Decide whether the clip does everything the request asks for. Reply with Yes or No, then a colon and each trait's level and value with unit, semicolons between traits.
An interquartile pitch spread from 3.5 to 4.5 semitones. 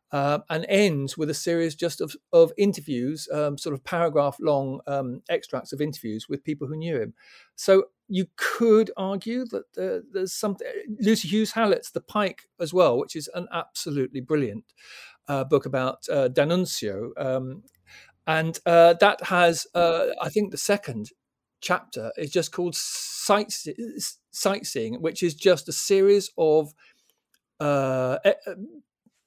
No: wide, 5.6 semitones